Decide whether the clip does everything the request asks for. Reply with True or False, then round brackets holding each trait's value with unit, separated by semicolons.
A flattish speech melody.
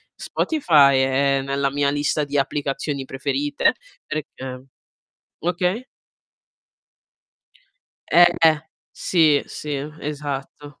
True (1.9 semitones)